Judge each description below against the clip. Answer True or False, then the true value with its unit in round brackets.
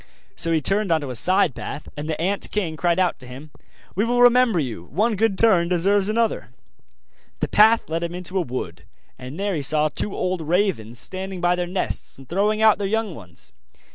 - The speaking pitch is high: False (180 Hz)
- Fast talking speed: True (210 wpm)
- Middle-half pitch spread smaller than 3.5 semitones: False (4.9 semitones)